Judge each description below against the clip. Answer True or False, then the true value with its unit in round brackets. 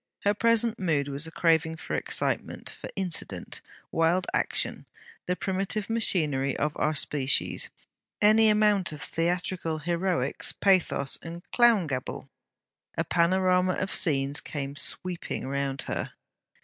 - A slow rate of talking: True (125 wpm)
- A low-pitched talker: False (170 Hz)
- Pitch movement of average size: True (4.5 semitones)